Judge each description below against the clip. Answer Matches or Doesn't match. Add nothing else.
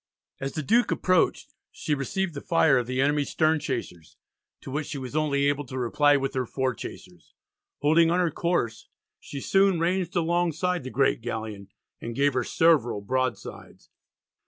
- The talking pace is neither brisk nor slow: Matches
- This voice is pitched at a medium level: Matches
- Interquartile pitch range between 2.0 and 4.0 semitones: Doesn't match